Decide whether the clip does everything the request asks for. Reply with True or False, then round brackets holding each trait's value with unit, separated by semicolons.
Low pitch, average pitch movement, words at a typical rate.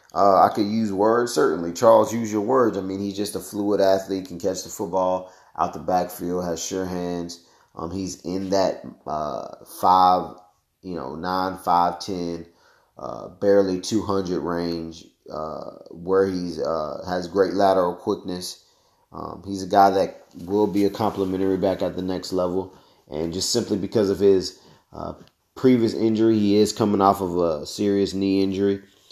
False (95 Hz; 1.9 semitones; 170 wpm)